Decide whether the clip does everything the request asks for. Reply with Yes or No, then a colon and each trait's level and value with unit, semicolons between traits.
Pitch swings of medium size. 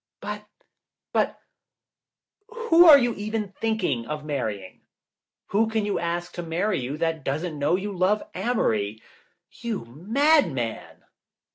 No: wide, 7.4 semitones